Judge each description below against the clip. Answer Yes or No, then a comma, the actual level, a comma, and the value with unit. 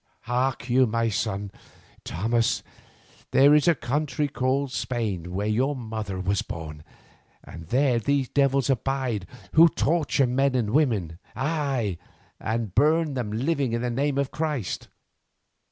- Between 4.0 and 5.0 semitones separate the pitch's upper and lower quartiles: Yes, average, 4.6 semitones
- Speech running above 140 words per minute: No, slow, 135 wpm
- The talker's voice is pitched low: Yes, low, 125 Hz